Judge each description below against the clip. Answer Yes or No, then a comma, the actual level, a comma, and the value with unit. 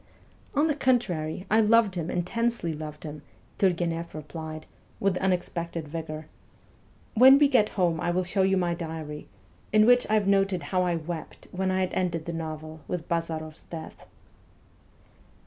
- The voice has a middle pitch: Yes, medium, 175 Hz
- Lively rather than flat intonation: No, average, 3.6 semitones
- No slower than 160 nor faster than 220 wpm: Yes, average, 170 wpm